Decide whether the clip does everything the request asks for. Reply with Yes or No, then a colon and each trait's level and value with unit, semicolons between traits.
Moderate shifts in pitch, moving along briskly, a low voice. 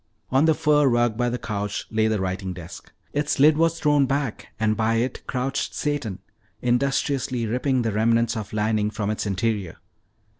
No: average, 4.3 semitones; average, 175 wpm; low, 115 Hz